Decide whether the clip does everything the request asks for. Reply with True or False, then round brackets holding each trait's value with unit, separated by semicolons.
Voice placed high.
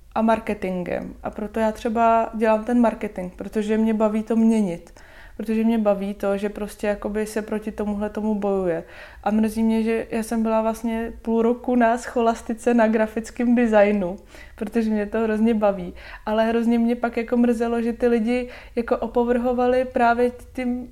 True (225 Hz)